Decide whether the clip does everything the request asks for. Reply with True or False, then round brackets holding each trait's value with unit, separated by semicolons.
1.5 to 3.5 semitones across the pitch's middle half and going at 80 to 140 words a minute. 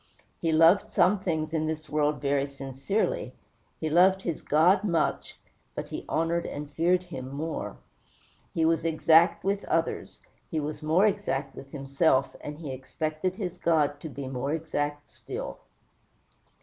False (2.7 semitones; 150 wpm)